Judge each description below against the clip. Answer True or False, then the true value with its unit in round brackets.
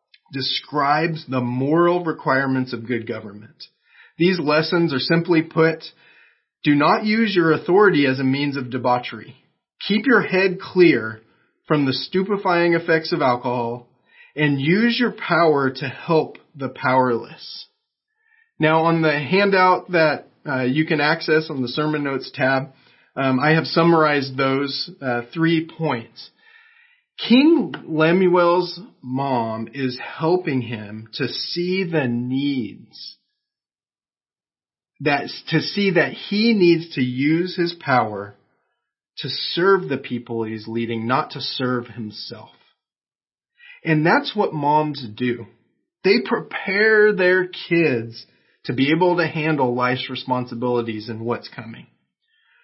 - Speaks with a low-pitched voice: False (150 Hz)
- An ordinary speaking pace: False (125 wpm)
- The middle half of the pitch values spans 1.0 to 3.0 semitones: False (5.5 semitones)